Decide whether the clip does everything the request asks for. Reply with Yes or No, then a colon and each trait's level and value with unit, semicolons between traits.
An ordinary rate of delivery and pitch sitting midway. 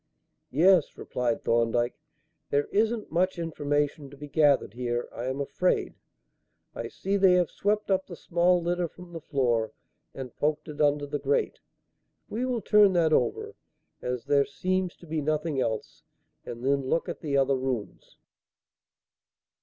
Yes: average, 155 wpm; medium, 150 Hz